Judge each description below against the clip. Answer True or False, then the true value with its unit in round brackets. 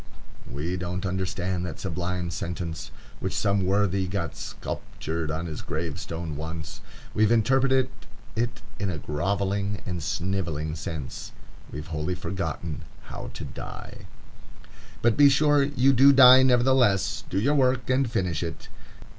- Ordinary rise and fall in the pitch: False (6.2 semitones)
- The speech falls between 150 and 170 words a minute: False (140 wpm)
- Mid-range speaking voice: False (95 Hz)